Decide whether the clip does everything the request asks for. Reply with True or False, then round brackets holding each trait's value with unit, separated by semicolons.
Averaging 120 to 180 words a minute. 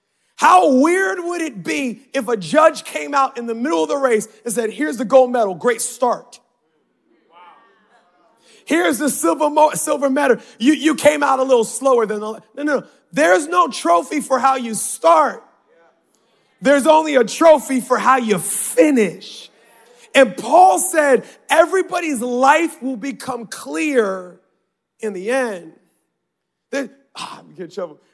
True (160 wpm)